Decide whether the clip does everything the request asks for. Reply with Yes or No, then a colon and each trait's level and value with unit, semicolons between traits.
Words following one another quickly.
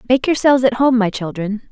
Yes: fast, 210 wpm